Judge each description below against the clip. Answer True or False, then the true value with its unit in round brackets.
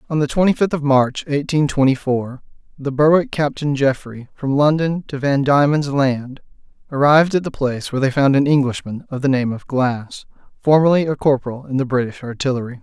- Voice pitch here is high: False (140 Hz)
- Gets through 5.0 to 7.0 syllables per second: True (5.5 syllables/s)